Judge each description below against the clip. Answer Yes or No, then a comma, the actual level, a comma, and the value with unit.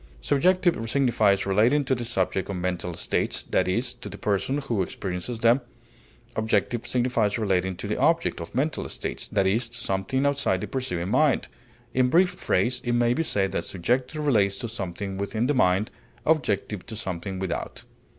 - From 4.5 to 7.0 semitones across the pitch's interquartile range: Yes, average, 5.2 semitones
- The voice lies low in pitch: Yes, low, 115 Hz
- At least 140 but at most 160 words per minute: No, average, 175 wpm